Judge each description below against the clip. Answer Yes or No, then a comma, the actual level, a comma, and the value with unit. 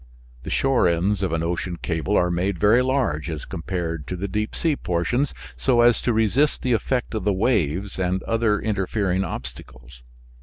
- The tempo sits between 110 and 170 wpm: No, average, 180 wpm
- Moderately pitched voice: No, very low, 95 Hz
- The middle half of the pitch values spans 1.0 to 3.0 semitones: No, average, 4.9 semitones